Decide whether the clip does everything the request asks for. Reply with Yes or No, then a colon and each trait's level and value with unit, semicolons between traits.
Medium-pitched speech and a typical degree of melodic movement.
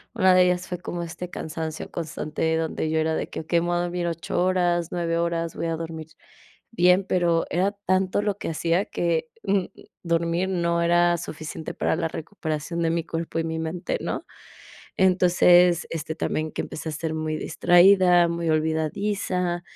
No: medium, 170 Hz; narrow, 1.8 semitones